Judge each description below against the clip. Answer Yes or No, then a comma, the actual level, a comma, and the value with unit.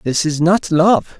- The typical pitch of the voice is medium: Yes, medium, 170 Hz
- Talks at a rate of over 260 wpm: No, average, 200 wpm